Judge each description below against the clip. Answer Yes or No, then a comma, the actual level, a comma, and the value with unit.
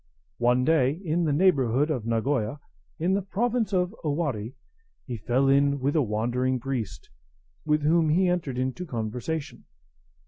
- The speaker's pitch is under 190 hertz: Yes, medium, 140 Hz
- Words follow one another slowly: No, average, 150 wpm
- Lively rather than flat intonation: No, average, 4.8 semitones